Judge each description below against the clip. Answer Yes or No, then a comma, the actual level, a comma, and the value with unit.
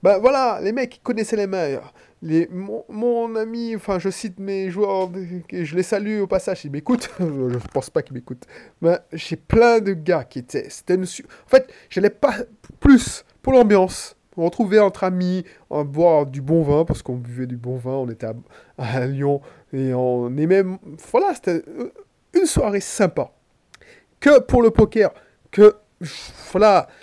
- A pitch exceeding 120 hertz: Yes, high, 190 Hz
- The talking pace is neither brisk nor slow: Yes, average, 180 wpm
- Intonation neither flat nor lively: No, wide, 6.4 semitones